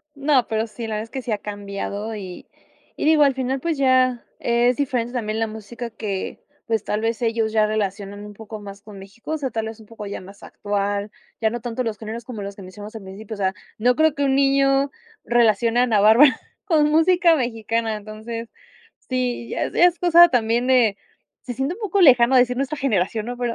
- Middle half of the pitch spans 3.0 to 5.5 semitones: Yes, average, 3.5 semitones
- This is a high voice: Yes, high, 230 Hz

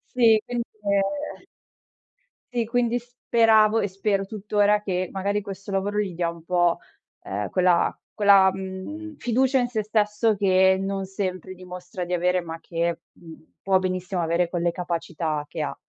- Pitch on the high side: Yes, high, 195 Hz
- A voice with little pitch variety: No, average, 3.0 semitones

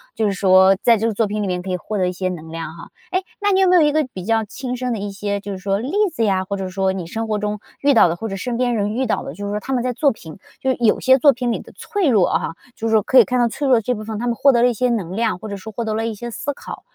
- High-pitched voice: Yes, high, 220 Hz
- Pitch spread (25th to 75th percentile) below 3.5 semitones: No, average, 4.1 semitones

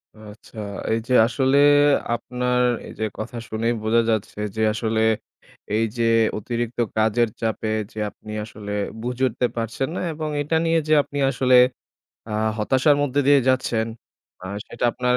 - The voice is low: Yes, low, 120 Hz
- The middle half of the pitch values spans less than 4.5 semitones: Yes, average, 2.8 semitones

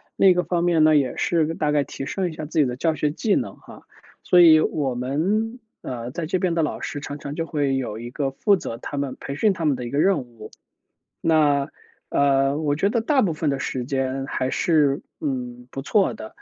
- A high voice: No, medium, 145 Hz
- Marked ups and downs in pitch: No, average, 3.9 semitones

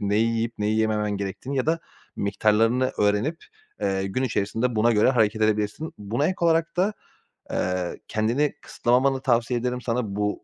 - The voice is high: No, low, 115 Hz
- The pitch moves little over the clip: No, average, 3.7 semitones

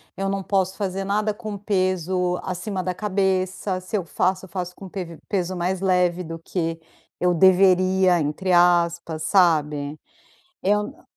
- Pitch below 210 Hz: Yes, medium, 185 Hz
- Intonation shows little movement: Yes, narrow, 1.8 semitones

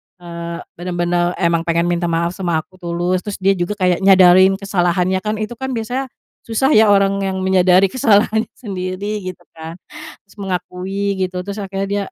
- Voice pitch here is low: No, medium, 185 Hz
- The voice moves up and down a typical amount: No, narrow, 2.3 semitones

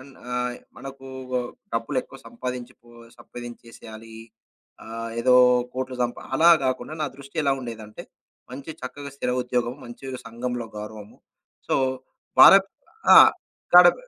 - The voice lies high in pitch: No, low, 125 Hz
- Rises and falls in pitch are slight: Yes, narrow, 2.3 semitones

